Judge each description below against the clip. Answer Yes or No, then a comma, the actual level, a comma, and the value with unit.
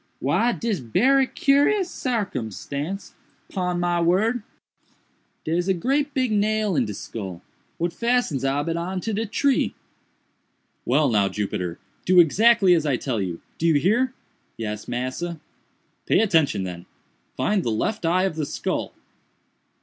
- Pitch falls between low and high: Yes, medium, 175 Hz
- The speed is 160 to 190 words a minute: No, slow, 135 wpm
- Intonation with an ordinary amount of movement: No, wide, 8.6 semitones